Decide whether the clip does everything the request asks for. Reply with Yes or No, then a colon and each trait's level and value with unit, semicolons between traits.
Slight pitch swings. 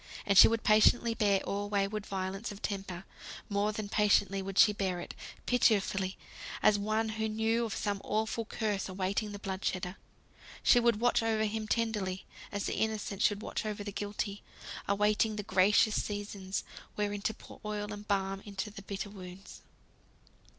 Yes: narrow, 1.7 semitones